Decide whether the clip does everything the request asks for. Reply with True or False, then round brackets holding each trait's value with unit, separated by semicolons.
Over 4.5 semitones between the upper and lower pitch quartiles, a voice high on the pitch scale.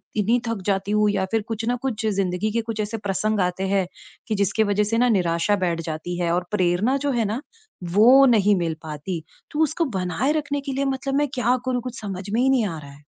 True (5.1 semitones; 210 Hz)